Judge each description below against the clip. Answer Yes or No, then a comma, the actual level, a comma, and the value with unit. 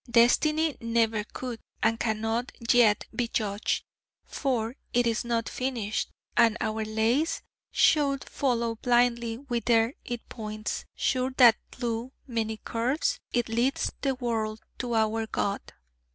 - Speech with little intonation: Yes, narrow, 1.9 semitones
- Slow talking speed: Yes, slow, 125 wpm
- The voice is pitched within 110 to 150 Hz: No, high, 235 Hz